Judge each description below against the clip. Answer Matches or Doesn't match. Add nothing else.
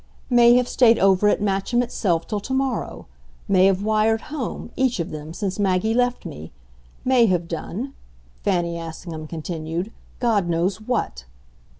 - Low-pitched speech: Doesn't match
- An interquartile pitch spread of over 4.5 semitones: Matches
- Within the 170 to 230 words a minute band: Doesn't match